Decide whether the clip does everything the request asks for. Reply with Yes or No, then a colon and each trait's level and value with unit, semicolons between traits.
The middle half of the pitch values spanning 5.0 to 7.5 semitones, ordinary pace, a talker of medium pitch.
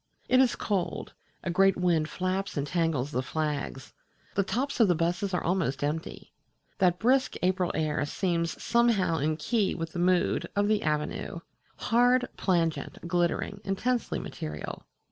No: average, 4.2 semitones; average, 150 wpm; medium, 180 Hz